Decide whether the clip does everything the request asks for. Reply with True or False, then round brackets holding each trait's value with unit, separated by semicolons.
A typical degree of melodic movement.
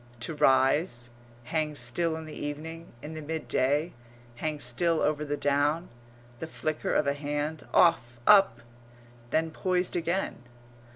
False (2.3 semitones)